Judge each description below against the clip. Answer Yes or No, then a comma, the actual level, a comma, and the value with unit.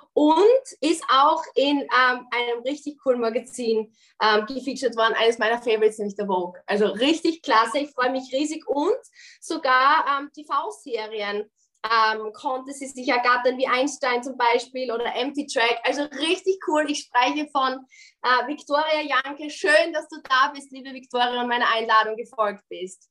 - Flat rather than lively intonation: No, average, 4.2 semitones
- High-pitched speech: Yes, very high, 255 Hz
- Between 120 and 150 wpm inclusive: No, average, 160 wpm